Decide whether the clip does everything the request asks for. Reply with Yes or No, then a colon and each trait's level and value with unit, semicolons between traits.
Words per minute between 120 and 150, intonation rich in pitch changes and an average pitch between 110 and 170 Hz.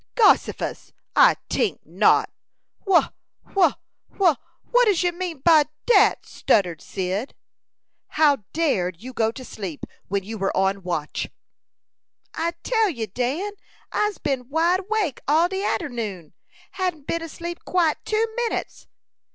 No: slow, 135 wpm; wide, 8.9 semitones; very high, 310 Hz